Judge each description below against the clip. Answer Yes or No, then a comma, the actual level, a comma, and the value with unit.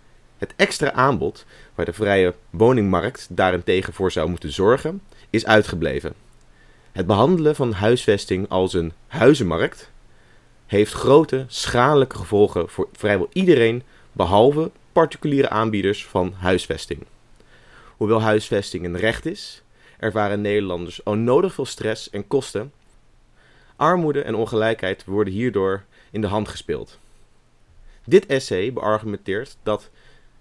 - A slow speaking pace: Yes, slow, 115 wpm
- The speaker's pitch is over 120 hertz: No, low, 105 Hz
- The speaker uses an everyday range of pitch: Yes, average, 4.8 semitones